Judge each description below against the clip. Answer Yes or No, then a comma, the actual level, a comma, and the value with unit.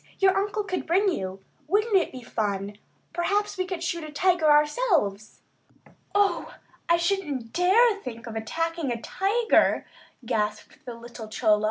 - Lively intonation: Yes, wide, 9.0 semitones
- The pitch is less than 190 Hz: No, very high, 330 Hz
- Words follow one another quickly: No, average, 165 wpm